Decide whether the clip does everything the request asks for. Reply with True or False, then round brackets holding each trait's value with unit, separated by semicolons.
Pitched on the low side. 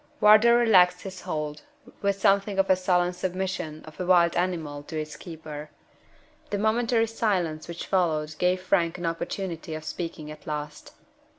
False (180 Hz)